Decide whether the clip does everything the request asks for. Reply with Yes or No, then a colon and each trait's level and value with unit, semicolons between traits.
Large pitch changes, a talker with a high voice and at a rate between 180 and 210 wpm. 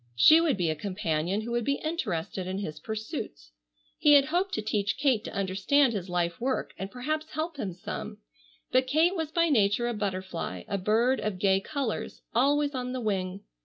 Yes: wide, 6.8 semitones; high, 220 Hz; average, 195 wpm